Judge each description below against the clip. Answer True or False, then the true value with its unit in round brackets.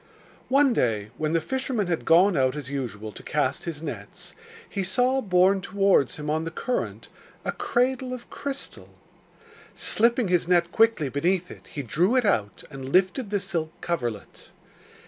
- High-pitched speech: False (180 Hz)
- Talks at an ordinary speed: True (165 wpm)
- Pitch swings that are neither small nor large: False (7.6 semitones)